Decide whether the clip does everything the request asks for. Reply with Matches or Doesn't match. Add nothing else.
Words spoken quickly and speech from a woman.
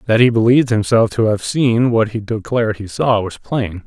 Doesn't match